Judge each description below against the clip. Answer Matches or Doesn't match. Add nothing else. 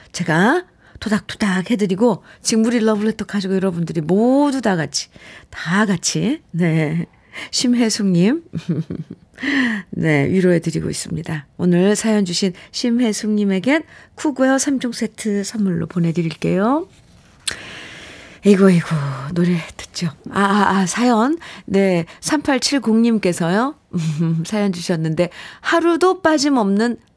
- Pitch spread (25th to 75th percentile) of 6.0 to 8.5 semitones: Doesn't match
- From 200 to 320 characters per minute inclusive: Matches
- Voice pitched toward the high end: Matches